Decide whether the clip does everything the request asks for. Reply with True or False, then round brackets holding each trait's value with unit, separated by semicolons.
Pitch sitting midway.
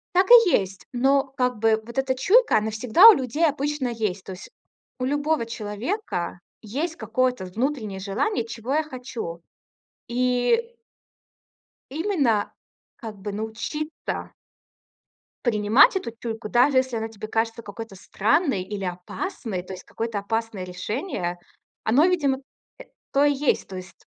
False (235 Hz)